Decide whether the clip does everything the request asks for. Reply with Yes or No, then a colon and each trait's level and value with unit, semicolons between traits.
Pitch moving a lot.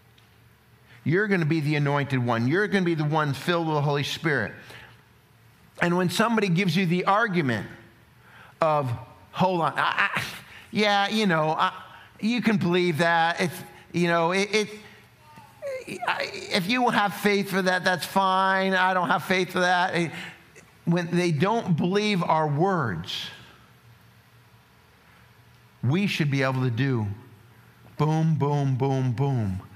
Yes: wide, 5.7 semitones